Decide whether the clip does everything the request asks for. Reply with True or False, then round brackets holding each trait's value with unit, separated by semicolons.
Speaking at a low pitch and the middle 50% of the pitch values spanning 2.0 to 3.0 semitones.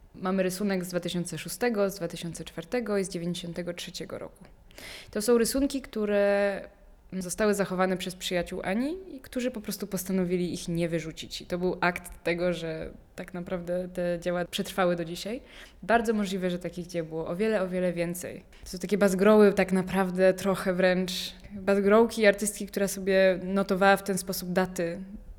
False (185 Hz; 2.4 semitones)